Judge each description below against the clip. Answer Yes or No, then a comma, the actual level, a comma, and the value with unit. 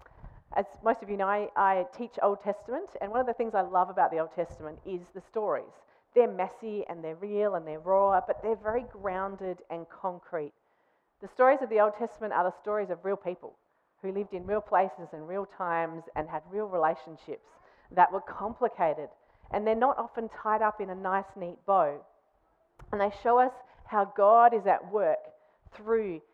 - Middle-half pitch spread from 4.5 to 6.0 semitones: No, average, 3.5 semitones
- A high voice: Yes, high, 200 Hz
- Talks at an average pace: Yes, average, 195 wpm